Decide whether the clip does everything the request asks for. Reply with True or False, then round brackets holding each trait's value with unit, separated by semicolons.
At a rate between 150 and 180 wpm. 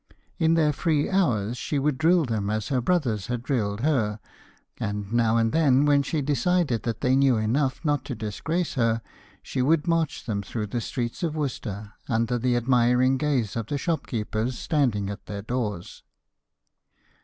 True (170 wpm)